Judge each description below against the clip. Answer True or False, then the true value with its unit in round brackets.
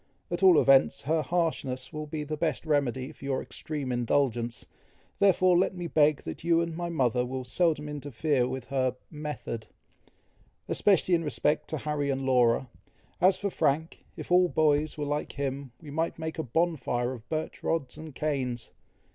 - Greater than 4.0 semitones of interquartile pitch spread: False (3.7 semitones)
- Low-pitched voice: False (150 Hz)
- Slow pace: False (170 wpm)